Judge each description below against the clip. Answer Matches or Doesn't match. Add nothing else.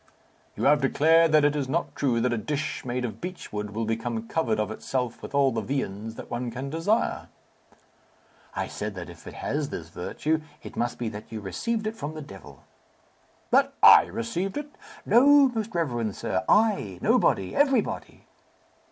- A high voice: Doesn't match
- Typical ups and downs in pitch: Doesn't match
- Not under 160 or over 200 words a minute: Matches